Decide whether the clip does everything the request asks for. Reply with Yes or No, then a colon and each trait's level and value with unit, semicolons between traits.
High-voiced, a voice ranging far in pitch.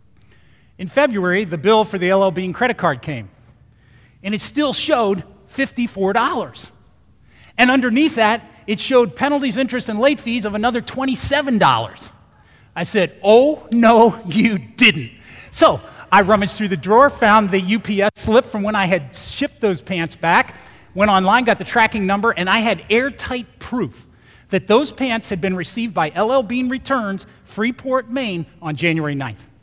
No: high, 210 Hz; average, 5.0 semitones